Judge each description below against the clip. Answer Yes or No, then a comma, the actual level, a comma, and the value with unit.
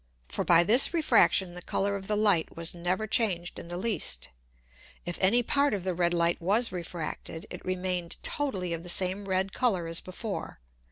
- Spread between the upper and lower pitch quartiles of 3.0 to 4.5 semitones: Yes, average, 3.3 semitones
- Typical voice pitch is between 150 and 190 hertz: Yes, medium, 185 Hz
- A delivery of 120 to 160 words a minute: No, average, 185 wpm